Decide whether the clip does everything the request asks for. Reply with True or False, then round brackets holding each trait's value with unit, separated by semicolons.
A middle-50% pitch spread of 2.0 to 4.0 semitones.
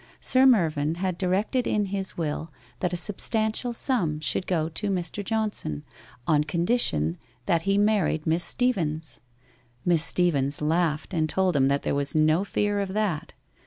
False (4.8 semitones)